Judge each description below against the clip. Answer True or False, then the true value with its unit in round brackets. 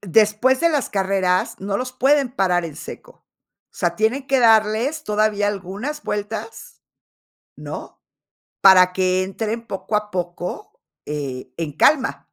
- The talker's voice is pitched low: False (210 Hz)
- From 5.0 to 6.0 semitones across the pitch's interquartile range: True (5.3 semitones)